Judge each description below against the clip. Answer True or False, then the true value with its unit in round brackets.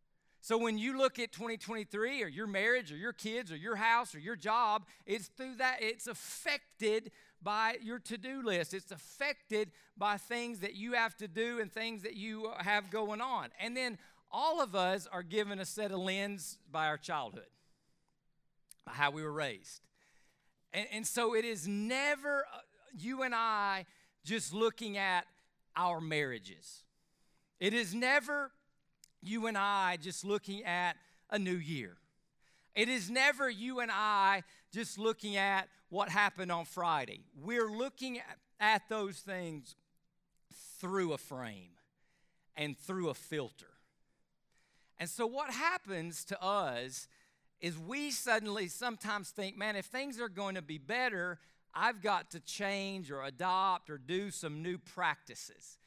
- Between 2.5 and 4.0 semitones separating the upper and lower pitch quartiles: False (4.7 semitones)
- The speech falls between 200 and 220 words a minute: False (155 wpm)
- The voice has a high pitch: True (200 Hz)